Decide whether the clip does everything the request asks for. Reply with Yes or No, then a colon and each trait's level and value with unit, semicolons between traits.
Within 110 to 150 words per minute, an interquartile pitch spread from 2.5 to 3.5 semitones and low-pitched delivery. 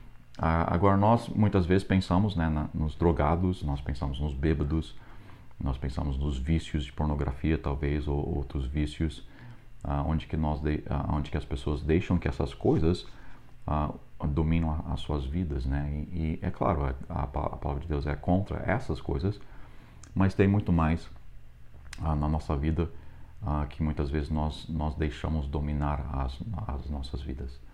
No: average, 165 wpm; average, 2.9 semitones; very low, 75 Hz